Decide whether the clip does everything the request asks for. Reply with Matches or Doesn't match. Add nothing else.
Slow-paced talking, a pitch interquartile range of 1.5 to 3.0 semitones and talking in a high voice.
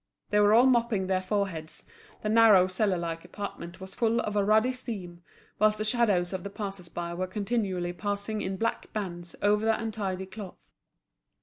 Doesn't match